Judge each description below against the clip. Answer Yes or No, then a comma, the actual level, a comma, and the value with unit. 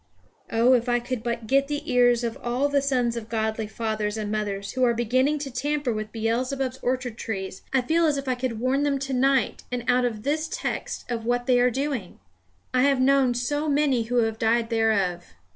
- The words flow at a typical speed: No, fast, 210 wpm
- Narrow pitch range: No, average, 3.2 semitones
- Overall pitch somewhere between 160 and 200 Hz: No, high, 245 Hz